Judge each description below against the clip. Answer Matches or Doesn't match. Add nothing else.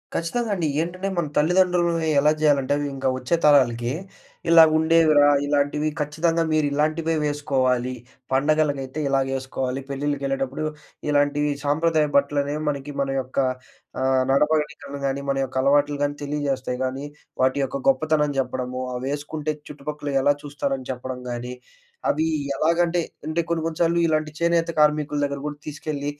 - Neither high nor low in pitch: Matches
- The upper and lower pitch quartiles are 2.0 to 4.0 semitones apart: Matches